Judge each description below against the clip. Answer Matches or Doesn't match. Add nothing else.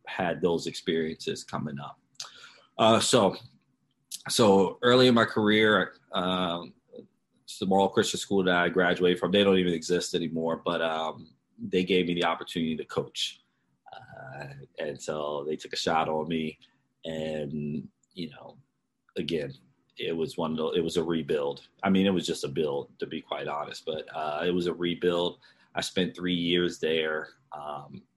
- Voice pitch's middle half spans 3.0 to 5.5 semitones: Doesn't match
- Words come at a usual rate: Matches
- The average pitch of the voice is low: Matches